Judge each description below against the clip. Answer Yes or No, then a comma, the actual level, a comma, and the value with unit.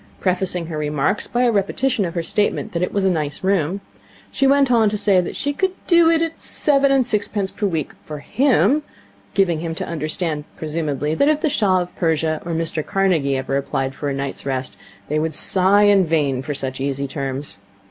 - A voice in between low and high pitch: Yes, medium, 170 Hz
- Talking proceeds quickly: Yes, fast, 210 wpm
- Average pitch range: No, wide, 5.9 semitones